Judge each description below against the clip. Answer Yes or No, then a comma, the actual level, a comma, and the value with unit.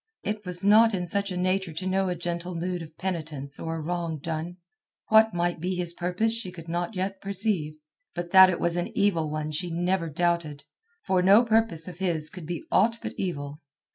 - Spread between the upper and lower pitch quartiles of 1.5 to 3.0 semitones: Yes, narrow, 2.5 semitones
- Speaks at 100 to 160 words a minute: No, fast, 205 wpm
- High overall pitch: No, medium, 175 Hz